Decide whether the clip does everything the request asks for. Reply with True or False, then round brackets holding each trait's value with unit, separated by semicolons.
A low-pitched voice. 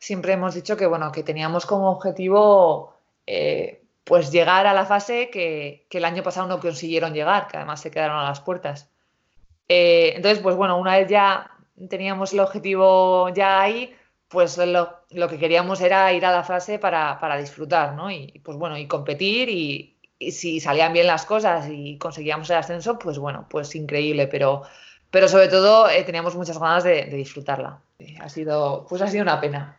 False (180 Hz)